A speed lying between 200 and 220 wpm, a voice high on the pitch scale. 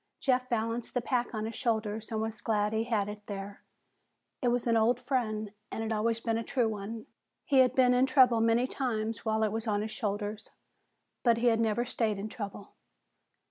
Yes: fast, 205 wpm; high, 225 Hz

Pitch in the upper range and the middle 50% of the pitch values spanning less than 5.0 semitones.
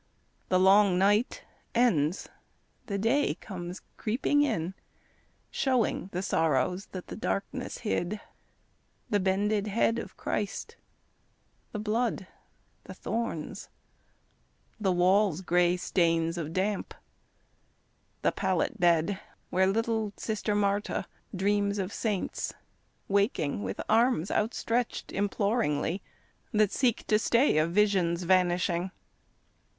Yes: high, 200 Hz; average, 3.3 semitones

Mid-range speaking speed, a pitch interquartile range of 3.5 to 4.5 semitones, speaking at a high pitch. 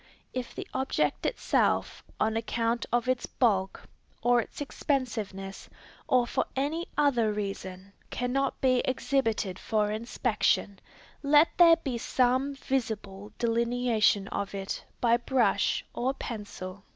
No: slow, 120 wpm; average, 3.9 semitones; high, 235 Hz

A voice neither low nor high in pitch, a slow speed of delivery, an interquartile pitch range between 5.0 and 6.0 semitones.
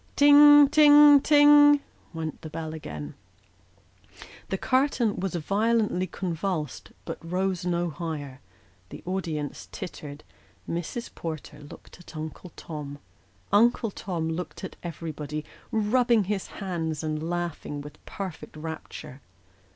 Yes: medium, 175 Hz; slow, 115 wpm; wide, 5.6 semitones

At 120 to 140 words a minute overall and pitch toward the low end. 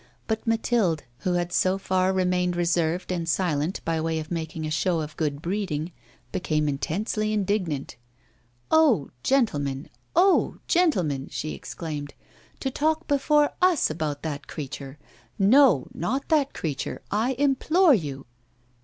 No: slow, 135 wpm; medium, 180 Hz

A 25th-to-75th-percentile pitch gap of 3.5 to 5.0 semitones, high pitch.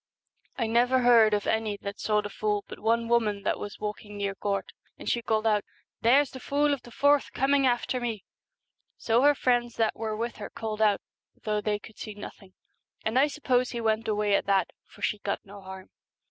No: average, 2.8 semitones; high, 220 Hz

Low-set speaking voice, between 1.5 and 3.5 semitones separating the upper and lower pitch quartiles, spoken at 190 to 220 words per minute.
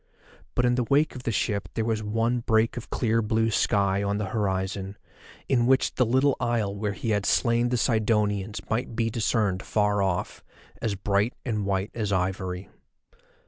No: low, 110 Hz; average, 2.8 semitones; average, 180 wpm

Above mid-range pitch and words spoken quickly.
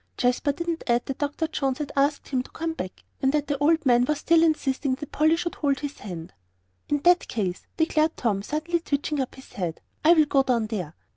Yes: very high, 285 Hz; fast, 220 wpm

